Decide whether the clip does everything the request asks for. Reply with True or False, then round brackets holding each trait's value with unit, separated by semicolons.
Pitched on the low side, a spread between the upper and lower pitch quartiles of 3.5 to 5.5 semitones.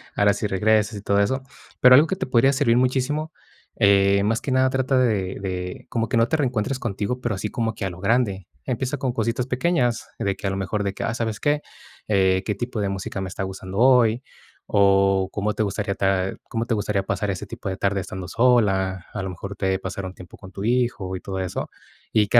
True (105 Hz; 4.1 semitones)